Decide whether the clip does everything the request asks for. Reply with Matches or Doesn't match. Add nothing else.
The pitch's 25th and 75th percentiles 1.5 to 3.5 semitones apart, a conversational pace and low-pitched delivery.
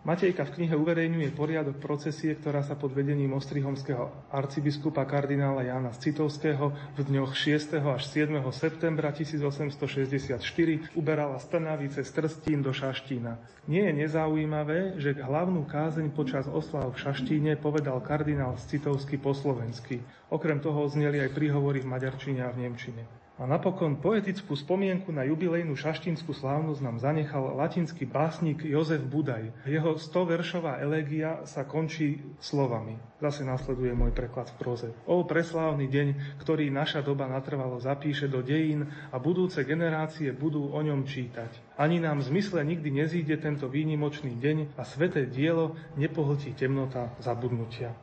Doesn't match